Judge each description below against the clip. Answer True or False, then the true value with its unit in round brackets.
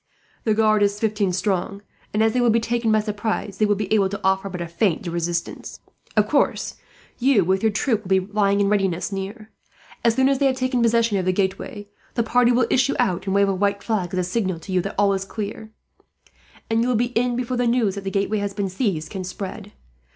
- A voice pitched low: False (205 Hz)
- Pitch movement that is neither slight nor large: True (3.1 semitones)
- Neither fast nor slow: False (240 wpm)